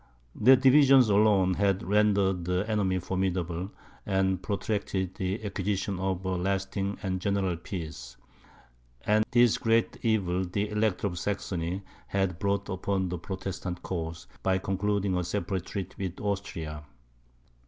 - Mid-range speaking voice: No, very low, 95 Hz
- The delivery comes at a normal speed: No, slow, 130 wpm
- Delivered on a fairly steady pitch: Yes, narrow, 1.9 semitones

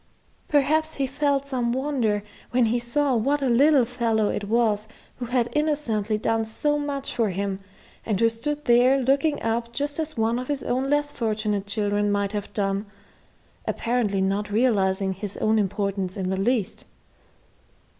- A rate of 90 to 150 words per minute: No, average, 165 wpm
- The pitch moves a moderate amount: Yes, average, 4.8 semitones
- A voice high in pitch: Yes, high, 235 Hz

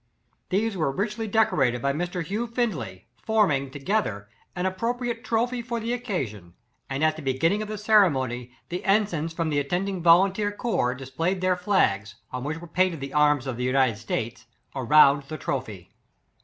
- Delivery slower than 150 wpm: No, average, 180 wpm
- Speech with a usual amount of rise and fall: No, wide, 7.5 semitones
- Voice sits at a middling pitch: Yes, medium, 165 Hz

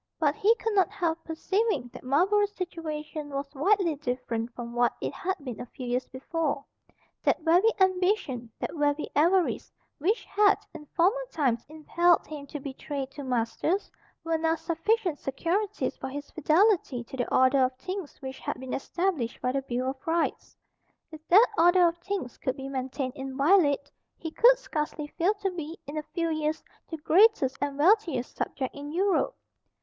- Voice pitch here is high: Yes, very high, 310 Hz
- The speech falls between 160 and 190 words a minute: Yes, average, 170 wpm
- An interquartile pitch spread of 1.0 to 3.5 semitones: No, average, 5.3 semitones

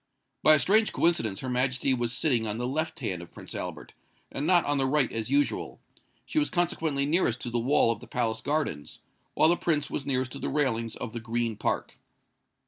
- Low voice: Yes, low, 130 Hz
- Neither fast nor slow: No, fast, 215 wpm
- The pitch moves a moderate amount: Yes, average, 4.6 semitones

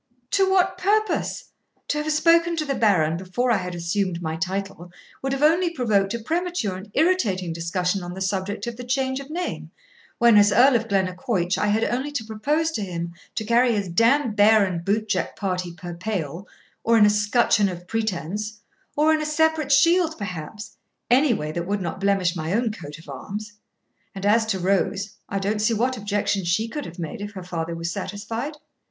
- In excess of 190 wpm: Yes, average, 200 wpm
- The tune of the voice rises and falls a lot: Yes, wide, 5.7 semitones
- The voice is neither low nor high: No, high, 210 Hz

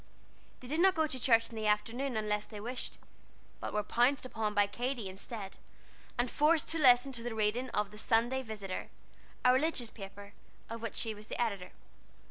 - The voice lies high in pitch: Yes, high, 230 Hz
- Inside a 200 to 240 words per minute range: No, average, 190 wpm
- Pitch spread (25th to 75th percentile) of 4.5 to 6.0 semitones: No, average, 3.4 semitones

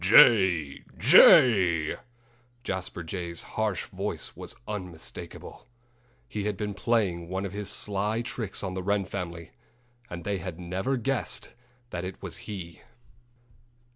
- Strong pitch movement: No, average, 3.2 semitones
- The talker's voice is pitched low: Yes, very low, 95 Hz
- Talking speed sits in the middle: No, slow, 130 wpm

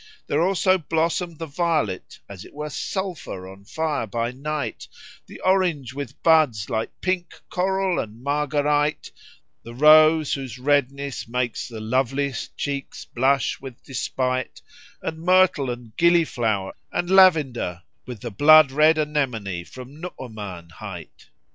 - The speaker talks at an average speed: No, slow, 130 wpm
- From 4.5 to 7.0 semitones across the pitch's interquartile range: Yes, average, 5.1 semitones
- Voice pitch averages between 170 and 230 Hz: No, medium, 140 Hz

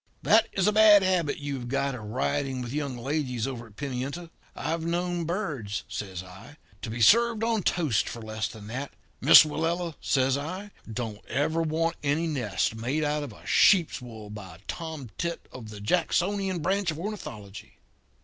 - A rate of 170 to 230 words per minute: Yes, average, 175 wpm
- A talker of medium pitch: Yes, medium, 145 Hz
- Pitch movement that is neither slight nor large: No, wide, 6.7 semitones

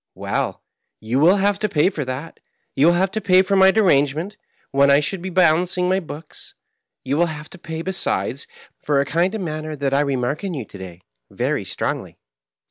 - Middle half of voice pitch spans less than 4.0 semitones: No, average, 5.0 semitones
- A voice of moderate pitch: Yes, medium, 165 Hz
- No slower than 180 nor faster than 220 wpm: Yes, fast, 205 wpm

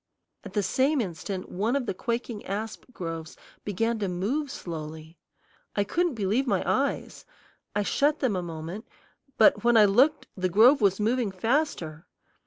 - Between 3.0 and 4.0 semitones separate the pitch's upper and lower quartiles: No, average, 5.1 semitones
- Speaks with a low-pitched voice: No, high, 210 Hz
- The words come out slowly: No, average, 160 wpm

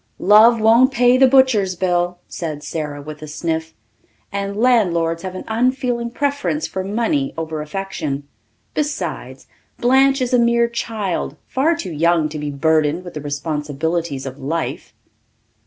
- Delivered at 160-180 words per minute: No, average, 145 wpm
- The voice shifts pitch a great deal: Yes, wide, 7.4 semitones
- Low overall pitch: No, medium, 185 Hz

